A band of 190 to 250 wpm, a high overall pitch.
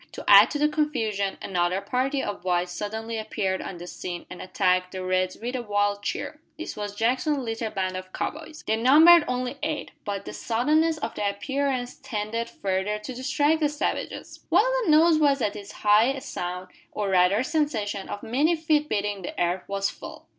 Yes: average, 195 wpm; high, 220 Hz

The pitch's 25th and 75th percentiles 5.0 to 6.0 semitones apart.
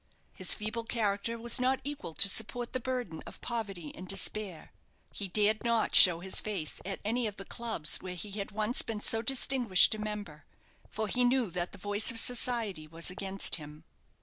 No: average, 3.8 semitones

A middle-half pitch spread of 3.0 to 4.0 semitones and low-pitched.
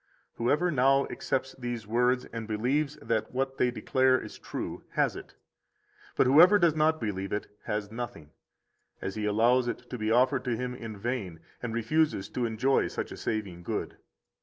Yes: average, 3.5 semitones; low, 120 Hz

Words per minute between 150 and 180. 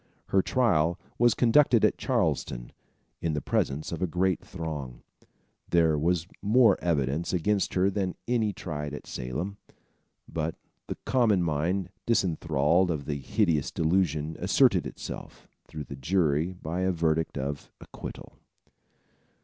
No: slow, 135 wpm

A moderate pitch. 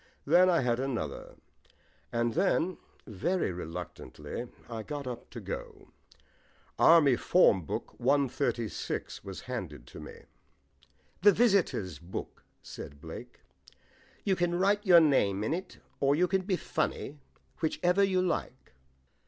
Yes: medium, 145 Hz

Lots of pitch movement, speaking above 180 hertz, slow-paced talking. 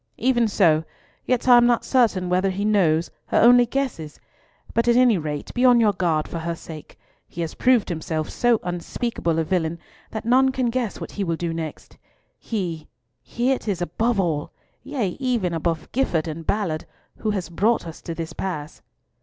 No: wide, 6.5 semitones; high, 190 Hz; average, 180 wpm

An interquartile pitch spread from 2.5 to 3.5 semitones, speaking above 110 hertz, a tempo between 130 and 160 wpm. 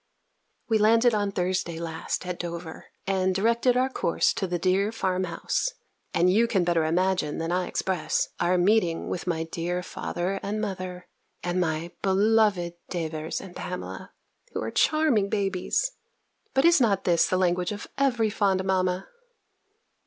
Yes: average, 3.2 semitones; medium, 185 Hz; average, 155 wpm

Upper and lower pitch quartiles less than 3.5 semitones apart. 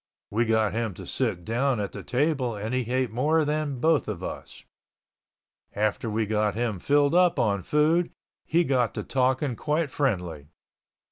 No: average, 5.3 semitones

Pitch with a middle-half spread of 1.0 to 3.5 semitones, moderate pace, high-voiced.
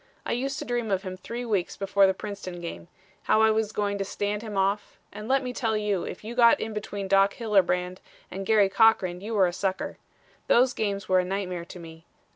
No: average, 2.8 semitones; fast, 225 wpm; high, 200 Hz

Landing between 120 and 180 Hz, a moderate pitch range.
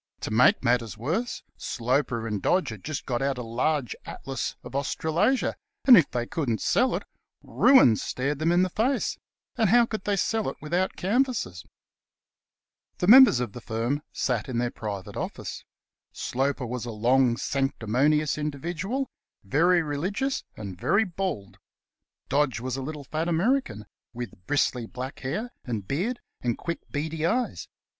No: medium, 140 Hz; wide, 7.2 semitones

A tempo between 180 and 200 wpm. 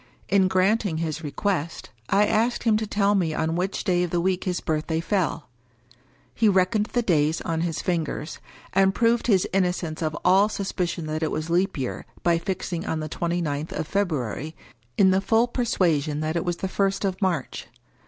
Yes: average, 190 wpm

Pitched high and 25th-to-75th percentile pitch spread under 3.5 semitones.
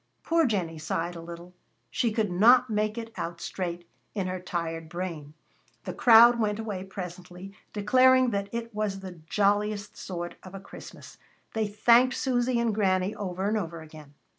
No: high, 200 Hz; average, 4.1 semitones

